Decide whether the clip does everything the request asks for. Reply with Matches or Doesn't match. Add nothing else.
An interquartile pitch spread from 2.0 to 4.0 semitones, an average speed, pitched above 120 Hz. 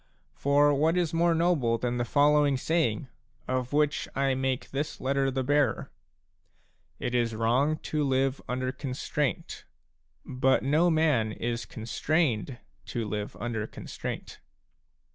Doesn't match